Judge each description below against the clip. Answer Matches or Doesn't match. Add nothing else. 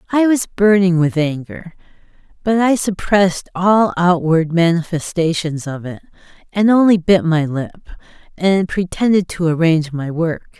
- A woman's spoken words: Matches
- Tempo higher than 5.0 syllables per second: Doesn't match